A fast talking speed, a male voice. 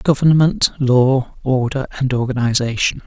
No: slow, 100 wpm; male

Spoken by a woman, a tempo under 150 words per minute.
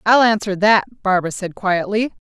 No: female; average, 155 wpm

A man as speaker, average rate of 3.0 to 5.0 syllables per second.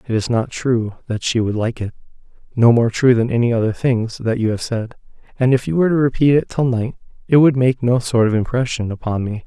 No: male; 5.8 syllables/s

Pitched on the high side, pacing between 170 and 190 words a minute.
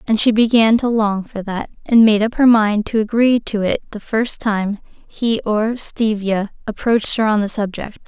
No: high, 220 Hz; average, 200 wpm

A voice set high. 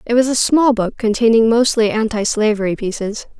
Yes: high, 225 Hz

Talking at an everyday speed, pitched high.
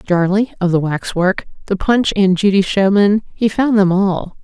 Yes: average, 175 wpm; high, 195 Hz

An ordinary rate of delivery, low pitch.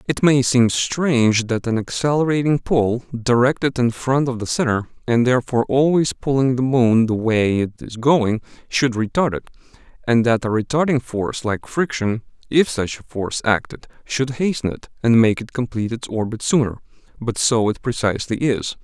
Yes: average, 175 wpm; low, 125 Hz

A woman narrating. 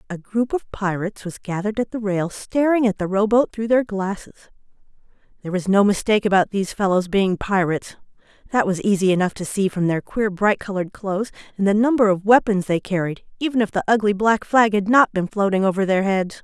Yes: female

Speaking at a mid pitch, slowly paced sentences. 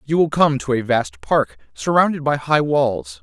No: medium, 150 Hz; fast, 205 wpm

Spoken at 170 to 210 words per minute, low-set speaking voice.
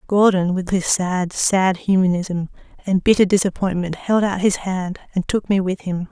No: average, 175 wpm; medium, 185 Hz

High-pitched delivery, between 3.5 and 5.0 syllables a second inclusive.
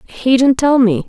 Yes: very high, 250 Hz; 4.4 syllables/s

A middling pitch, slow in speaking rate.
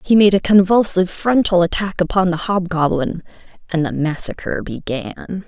Yes: medium, 180 Hz; slow, 130 wpm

